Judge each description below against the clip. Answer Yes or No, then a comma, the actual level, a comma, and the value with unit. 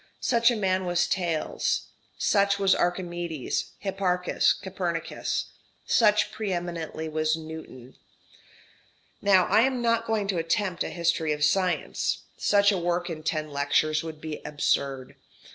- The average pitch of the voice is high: No, medium, 175 Hz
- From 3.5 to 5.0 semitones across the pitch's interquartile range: Yes, average, 3.9 semitones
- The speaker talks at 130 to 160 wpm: Yes, slow, 135 wpm